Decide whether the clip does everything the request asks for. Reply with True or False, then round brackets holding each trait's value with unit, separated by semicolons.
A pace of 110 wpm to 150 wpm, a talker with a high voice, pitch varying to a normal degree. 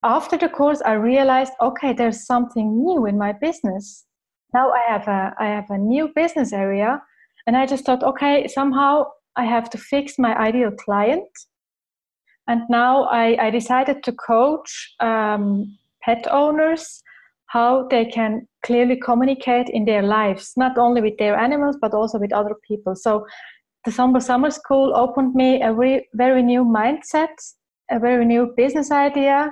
False (165 wpm; 245 Hz; 3.7 semitones)